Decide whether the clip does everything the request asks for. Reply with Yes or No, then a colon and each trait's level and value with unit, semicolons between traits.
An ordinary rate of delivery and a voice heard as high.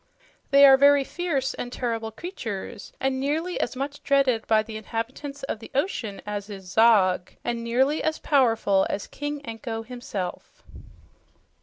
Yes: average, 150 wpm; high, 245 Hz